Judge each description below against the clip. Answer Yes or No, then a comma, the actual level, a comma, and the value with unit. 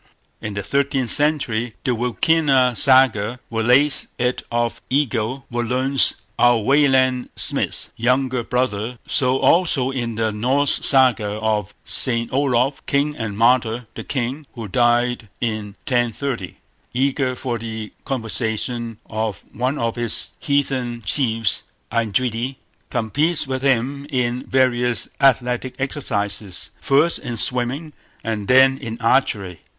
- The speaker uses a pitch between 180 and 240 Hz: No, low, 125 Hz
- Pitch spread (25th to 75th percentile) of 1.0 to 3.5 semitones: Yes, average, 2.8 semitones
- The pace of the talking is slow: Yes, slow, 115 wpm